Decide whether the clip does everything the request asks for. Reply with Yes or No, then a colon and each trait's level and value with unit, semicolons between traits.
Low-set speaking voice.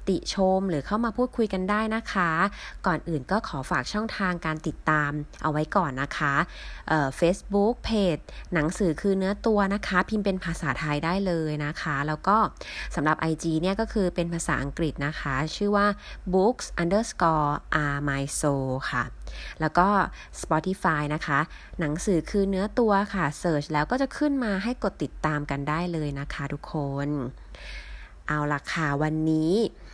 No: medium, 170 Hz